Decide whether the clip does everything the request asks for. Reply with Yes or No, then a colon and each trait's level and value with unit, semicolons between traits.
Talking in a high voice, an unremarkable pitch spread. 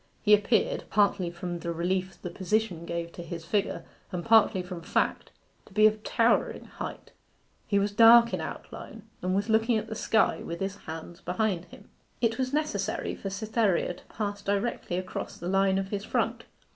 Yes: high, 200 Hz; average, 3.4 semitones